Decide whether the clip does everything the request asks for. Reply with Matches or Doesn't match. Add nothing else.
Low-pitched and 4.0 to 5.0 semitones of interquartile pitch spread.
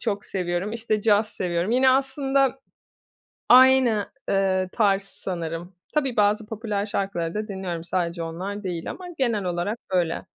Doesn't match